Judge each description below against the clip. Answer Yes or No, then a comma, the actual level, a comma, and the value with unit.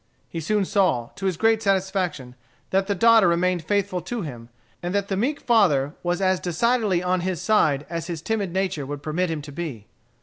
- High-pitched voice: No, medium, 180 Hz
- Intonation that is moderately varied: Yes, average, 4.0 semitones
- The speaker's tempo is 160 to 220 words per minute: Yes, average, 200 wpm